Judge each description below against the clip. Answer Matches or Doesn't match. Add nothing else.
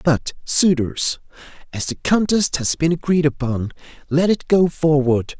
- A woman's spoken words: Doesn't match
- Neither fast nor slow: Matches